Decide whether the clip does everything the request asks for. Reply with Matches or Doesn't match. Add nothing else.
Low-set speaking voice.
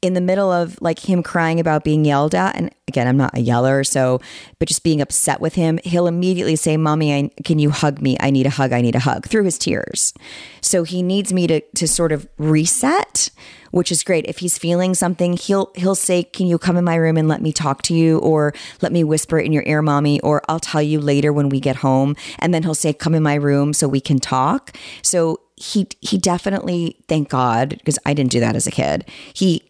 Doesn't match